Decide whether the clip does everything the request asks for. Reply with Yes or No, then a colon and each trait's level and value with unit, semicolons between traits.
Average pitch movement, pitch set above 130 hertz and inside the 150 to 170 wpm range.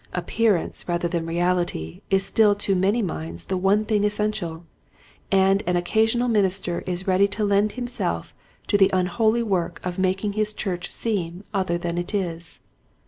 Yes: average, 3.0 semitones; high, 190 Hz; average, 160 wpm